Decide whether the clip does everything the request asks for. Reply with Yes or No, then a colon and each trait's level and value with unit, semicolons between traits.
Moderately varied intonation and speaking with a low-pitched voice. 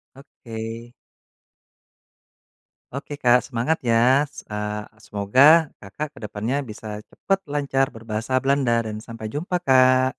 Yes: average, 4.0 semitones; low, 125 Hz